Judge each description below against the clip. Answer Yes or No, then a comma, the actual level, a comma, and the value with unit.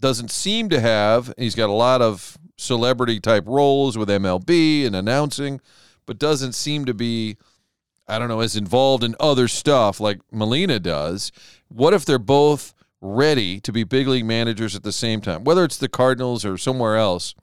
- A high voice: No, low, 120 Hz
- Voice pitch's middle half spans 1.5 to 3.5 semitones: No, average, 4.2 semitones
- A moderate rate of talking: Yes, average, 185 wpm